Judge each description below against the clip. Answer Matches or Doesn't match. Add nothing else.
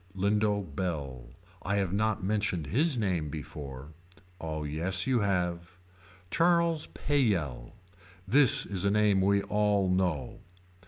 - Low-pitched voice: Matches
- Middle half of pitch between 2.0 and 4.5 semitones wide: Doesn't match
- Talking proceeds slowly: Matches